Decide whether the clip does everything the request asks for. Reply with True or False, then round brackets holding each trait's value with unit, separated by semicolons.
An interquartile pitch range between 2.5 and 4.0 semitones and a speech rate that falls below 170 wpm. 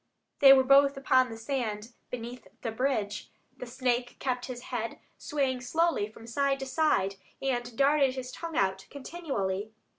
True (3.3 semitones; 155 wpm)